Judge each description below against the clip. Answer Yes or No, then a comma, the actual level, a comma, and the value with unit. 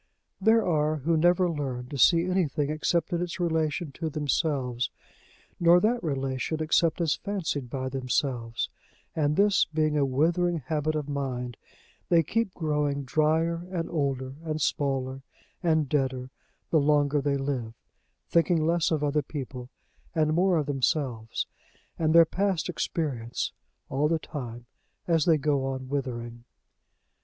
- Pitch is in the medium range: Yes, medium, 150 Hz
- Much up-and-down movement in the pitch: No, average, 3.7 semitones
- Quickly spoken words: No, average, 145 wpm